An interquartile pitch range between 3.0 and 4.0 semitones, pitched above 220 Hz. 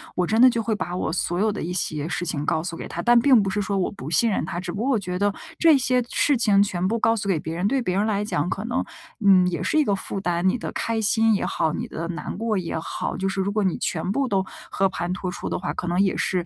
No: average, 3.7 semitones; high, 195 Hz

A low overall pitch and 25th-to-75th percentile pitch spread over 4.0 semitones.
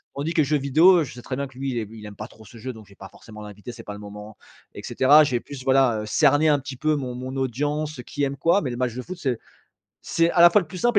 Yes: low, 130 Hz; average, 4.7 semitones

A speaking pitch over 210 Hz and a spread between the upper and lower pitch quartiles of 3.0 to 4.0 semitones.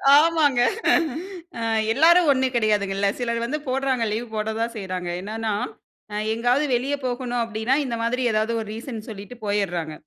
Yes: high, 230 Hz; average, 3.4 semitones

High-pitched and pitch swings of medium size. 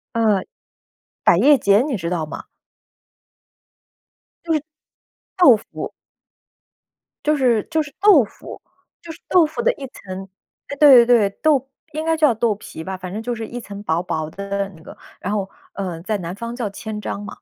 No: high, 220 Hz; wide, 6.1 semitones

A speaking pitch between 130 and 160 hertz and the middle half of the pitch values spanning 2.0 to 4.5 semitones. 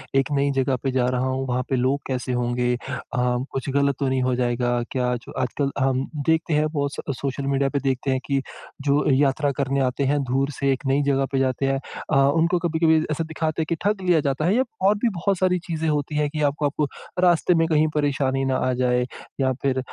Yes: medium, 140 Hz; narrow, 2.6 semitones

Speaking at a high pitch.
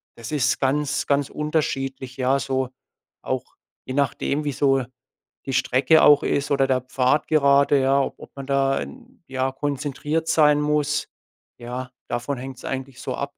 No: medium, 140 Hz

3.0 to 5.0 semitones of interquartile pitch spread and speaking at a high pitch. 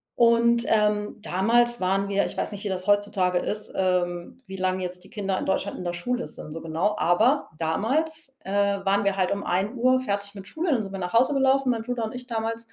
Yes: average, 4.0 semitones; high, 205 Hz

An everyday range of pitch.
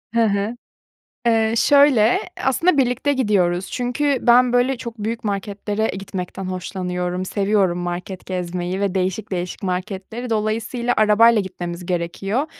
Yes: average, 4.3 semitones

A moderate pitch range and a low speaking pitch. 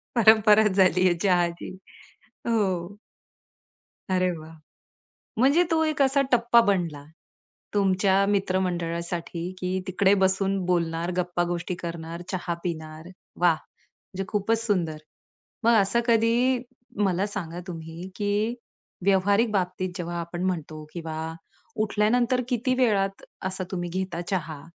No: average, 3.4 semitones; medium, 185 Hz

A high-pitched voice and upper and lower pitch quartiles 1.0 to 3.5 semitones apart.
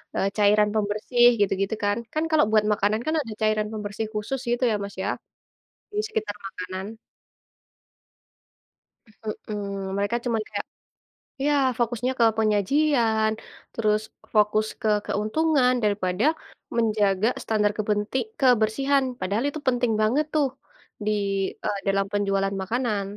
Yes: high, 215 Hz; average, 2.9 semitones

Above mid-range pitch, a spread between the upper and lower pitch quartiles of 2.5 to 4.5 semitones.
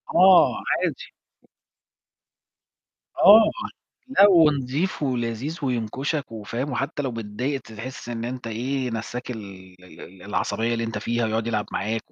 No: low, 120 Hz; average, 3.9 semitones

